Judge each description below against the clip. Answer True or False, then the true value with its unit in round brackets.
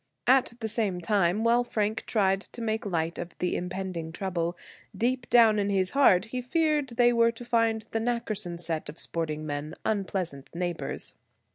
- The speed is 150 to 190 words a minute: True (170 wpm)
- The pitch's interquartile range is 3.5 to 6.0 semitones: True (5.0 semitones)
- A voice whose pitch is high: True (205 Hz)